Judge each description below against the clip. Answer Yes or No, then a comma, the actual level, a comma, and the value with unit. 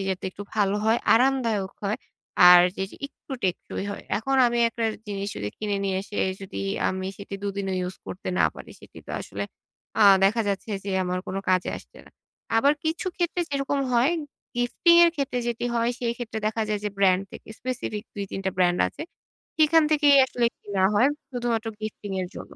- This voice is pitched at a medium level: No, high, 215 Hz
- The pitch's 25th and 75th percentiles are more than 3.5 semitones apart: Yes, average, 4.2 semitones